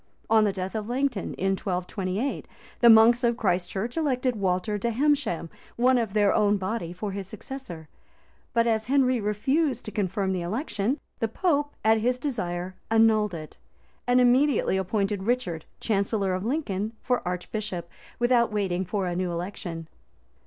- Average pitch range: Yes, average, 4.5 semitones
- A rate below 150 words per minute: No, average, 160 wpm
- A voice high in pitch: Yes, high, 215 Hz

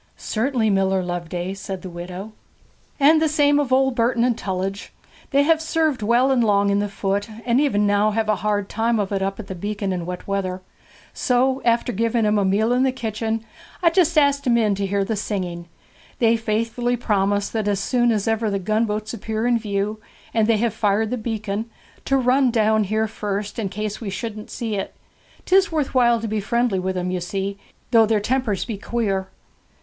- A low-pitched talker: No, high, 215 Hz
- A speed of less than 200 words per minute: No, fast, 205 wpm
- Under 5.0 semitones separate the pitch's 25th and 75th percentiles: Yes, average, 3.2 semitones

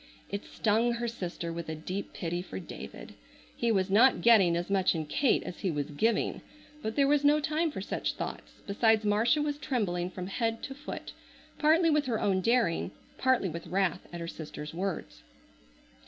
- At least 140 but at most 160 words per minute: No, average, 185 wpm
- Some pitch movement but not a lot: No, wide, 5.9 semitones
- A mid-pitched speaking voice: No, high, 205 Hz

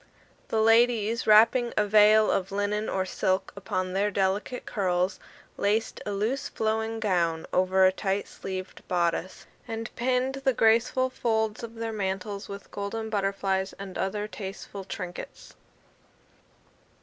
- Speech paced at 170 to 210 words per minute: No, slow, 135 wpm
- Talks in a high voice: Yes, high, 205 Hz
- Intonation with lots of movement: No, average, 2.8 semitones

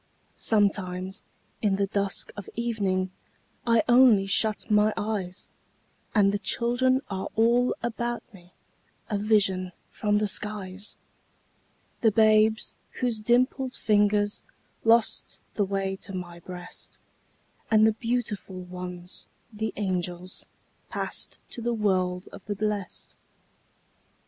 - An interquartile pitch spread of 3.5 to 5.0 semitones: No, average, 2.8 semitones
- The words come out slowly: Yes, slow, 115 wpm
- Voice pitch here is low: No, high, 205 Hz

